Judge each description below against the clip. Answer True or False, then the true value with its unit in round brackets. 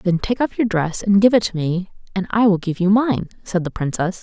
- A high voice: True (195 Hz)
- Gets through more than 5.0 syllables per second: True (5.3 syllables/s)